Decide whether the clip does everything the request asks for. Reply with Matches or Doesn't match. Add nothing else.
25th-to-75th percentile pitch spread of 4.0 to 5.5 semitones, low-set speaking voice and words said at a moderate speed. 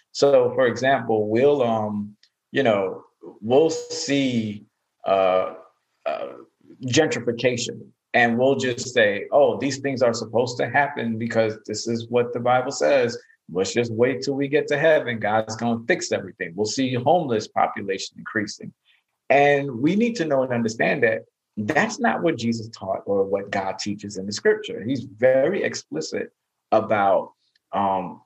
Matches